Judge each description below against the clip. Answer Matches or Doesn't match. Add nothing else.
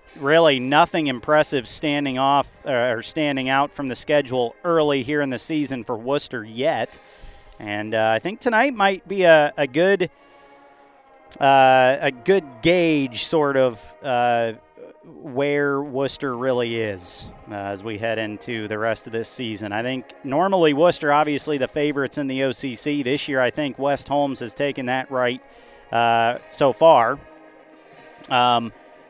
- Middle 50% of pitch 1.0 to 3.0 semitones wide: Doesn't match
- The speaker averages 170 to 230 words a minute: Doesn't match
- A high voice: Doesn't match